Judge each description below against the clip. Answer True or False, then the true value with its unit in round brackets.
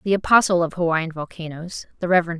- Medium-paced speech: True (175 wpm)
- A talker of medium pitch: True (170 Hz)